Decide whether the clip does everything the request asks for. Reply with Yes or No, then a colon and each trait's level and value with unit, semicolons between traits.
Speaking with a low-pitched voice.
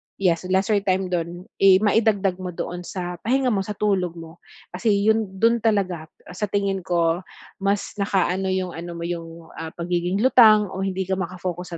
No: medium, 185 Hz